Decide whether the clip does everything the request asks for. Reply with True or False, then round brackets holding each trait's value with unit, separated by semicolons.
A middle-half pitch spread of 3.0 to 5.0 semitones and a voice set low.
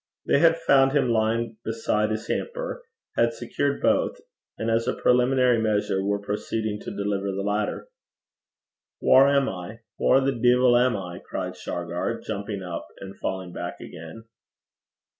True (4.0 semitones; 110 Hz)